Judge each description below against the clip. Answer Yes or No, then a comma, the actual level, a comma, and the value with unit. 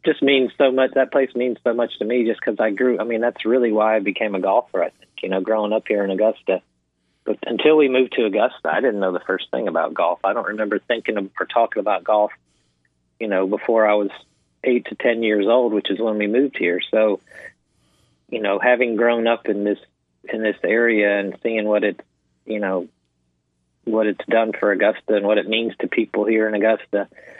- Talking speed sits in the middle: No, fast, 225 wpm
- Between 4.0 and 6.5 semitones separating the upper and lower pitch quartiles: No, average, 2.8 semitones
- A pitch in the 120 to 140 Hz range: No, low, 110 Hz